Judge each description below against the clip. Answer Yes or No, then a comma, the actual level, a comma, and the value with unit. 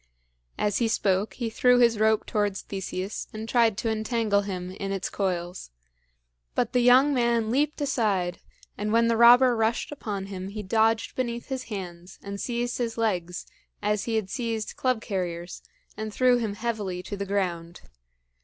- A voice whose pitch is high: Yes, high, 215 Hz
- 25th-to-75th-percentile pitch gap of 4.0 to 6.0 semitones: No, average, 3.3 semitones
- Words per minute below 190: Yes, average, 170 wpm